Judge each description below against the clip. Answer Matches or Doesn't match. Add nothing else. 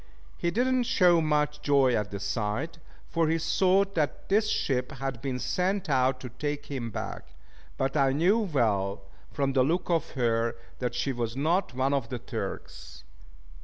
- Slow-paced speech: Doesn't match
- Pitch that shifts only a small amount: Doesn't match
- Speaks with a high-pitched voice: Doesn't match